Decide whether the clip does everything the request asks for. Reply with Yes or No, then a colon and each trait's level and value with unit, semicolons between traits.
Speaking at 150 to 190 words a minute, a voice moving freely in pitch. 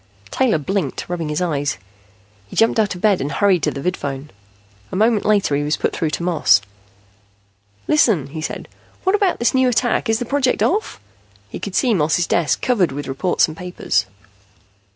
Yes: average, 185 wpm; wide, 7.1 semitones